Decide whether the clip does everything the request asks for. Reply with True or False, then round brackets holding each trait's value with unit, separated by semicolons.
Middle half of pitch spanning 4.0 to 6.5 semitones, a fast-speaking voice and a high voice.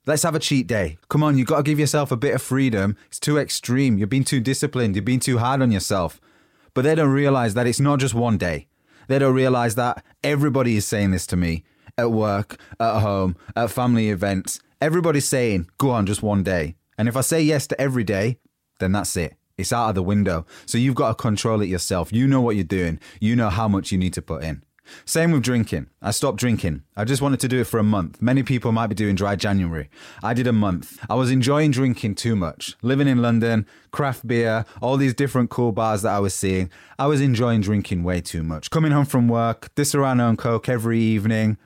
False (4.8 semitones; 235 wpm; 115 Hz)